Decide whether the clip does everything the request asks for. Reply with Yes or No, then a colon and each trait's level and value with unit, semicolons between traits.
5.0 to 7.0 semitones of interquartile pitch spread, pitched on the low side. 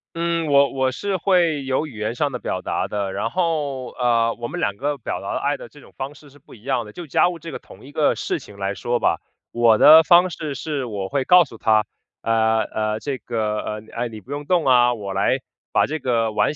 Yes: average, 5.3 semitones; low, 130 Hz